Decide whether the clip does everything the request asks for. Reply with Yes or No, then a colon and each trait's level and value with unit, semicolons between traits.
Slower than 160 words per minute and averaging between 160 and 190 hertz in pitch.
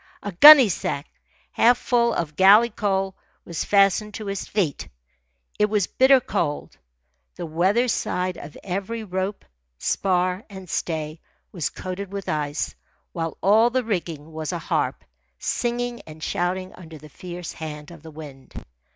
Yes: average, 145 wpm; medium, 185 Hz